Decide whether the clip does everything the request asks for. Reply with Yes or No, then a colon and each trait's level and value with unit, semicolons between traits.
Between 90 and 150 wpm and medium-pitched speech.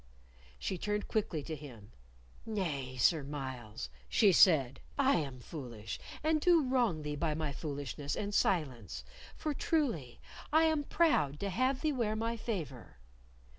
Yes: average, 145 wpm; medium, 160 Hz